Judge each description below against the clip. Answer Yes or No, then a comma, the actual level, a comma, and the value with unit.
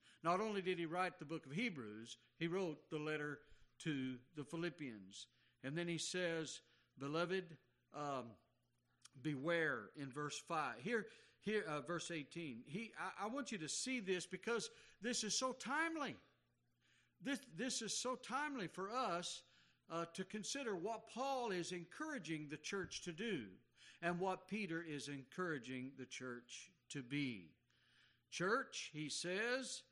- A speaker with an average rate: Yes, average, 150 wpm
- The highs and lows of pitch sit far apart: Yes, wide, 6.7 semitones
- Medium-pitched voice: Yes, medium, 170 Hz